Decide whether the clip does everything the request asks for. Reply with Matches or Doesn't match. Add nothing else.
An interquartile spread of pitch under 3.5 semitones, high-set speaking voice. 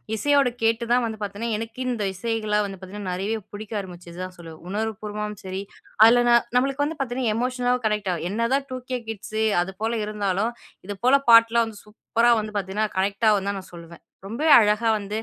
Matches